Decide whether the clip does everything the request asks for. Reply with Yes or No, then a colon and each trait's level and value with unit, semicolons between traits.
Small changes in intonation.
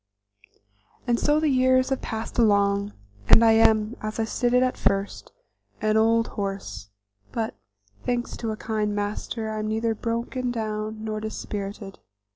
Yes: narrow, 1.8 semitones